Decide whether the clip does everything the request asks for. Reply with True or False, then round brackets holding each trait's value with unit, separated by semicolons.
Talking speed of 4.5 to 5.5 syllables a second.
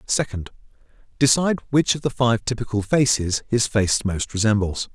True (5.1 syllables/s)